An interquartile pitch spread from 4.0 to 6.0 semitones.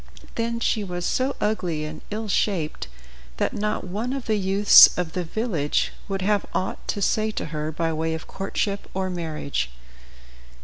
Yes: average, 4.7 semitones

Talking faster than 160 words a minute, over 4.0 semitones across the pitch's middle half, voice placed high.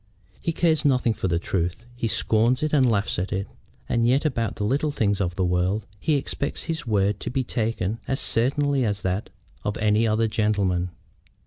No: average, 190 wpm; average, 4.7 semitones; low, 110 Hz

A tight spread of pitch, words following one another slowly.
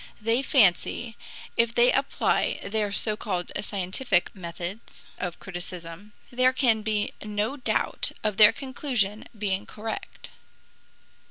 No: average, 3.8 semitones; slow, 115 wpm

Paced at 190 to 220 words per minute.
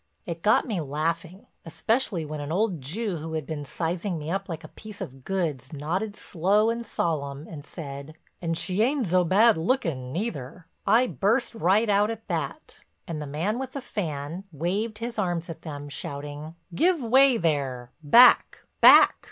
No: average, 170 wpm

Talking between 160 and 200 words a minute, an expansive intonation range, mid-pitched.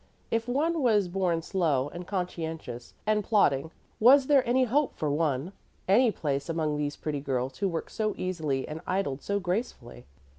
Yes: average, 170 wpm; wide, 6.6 semitones; medium, 175 Hz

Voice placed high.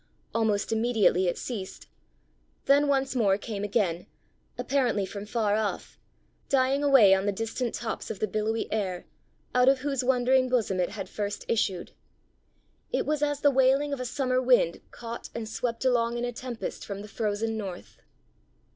Yes: high, 230 Hz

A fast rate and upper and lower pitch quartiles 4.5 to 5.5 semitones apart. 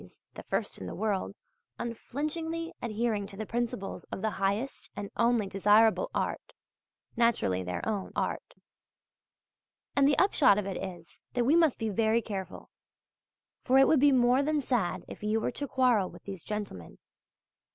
No: average, 165 wpm; average, 4.8 semitones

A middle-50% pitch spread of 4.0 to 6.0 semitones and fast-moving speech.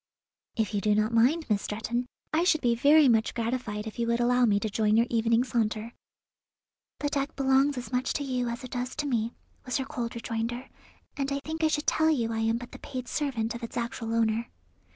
No: average, 3.0 semitones; fast, 225 wpm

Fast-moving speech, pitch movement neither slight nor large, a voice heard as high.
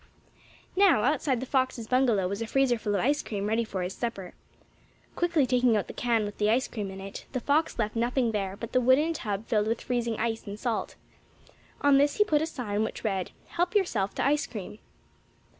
Yes: fast, 210 wpm; average, 4.3 semitones; high, 235 Hz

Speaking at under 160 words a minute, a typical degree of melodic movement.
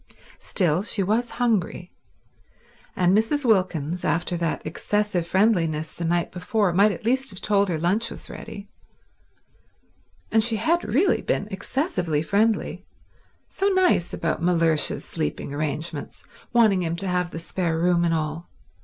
Yes: average, 140 wpm; average, 4.7 semitones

